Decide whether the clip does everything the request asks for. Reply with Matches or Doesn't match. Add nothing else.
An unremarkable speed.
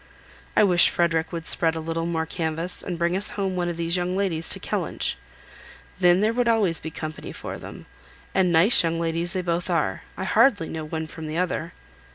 Doesn't match